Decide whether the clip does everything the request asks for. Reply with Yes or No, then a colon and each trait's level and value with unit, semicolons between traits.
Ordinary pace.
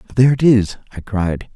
Yes: average, 195 wpm